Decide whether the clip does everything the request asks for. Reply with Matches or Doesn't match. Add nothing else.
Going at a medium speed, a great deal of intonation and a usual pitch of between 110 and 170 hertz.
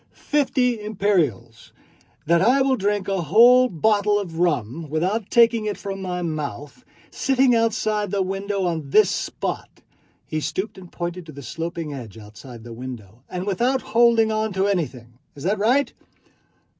Doesn't match